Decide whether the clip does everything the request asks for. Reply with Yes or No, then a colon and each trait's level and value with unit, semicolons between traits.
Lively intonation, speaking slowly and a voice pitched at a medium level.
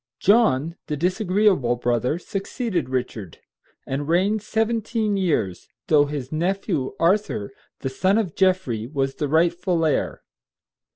Yes: wide, 6.6 semitones; slow, 120 wpm; medium, 170 Hz